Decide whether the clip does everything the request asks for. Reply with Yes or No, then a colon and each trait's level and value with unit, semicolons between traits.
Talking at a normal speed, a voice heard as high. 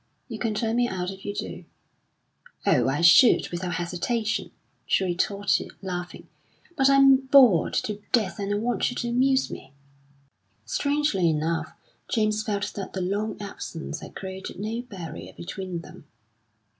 Yes: average, 150 wpm; high, 205 Hz